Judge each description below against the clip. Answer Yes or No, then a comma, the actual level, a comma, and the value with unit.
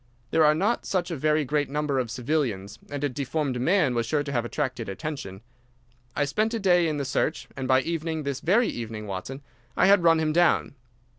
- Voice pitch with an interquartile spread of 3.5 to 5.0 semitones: Yes, average, 4.3 semitones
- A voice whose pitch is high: No, medium, 145 Hz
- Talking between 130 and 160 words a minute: No, average, 200 wpm